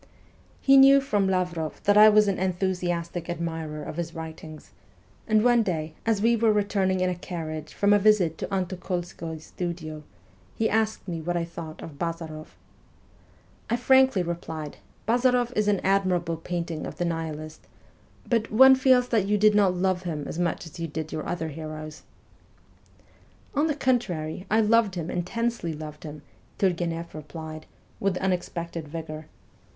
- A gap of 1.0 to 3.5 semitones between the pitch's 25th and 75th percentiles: No, average, 4.5 semitones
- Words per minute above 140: Yes, average, 165 wpm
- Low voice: No, medium, 175 Hz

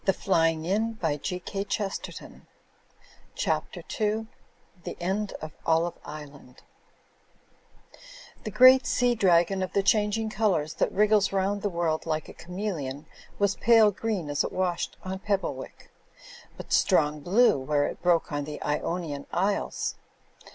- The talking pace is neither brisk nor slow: No, slow, 130 wpm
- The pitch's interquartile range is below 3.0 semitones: No, average, 4.8 semitones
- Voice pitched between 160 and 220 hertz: Yes, medium, 185 Hz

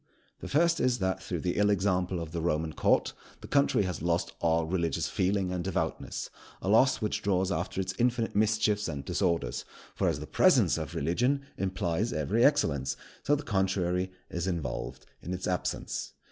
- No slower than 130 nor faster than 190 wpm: Yes, average, 175 wpm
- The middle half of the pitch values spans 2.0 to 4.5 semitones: Yes, average, 3.6 semitones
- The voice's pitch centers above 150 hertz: No, very low, 95 Hz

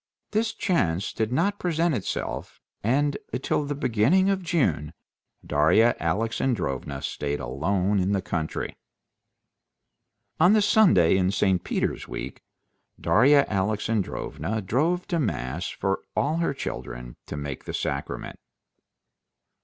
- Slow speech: Yes, slow, 120 wpm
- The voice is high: No, low, 105 Hz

